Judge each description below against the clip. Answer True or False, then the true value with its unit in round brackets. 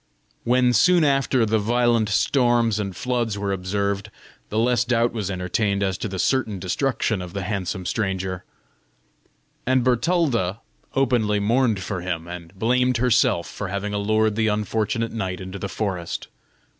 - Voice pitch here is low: True (110 Hz)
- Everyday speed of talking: True (150 wpm)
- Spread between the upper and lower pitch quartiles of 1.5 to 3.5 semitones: False (3.9 semitones)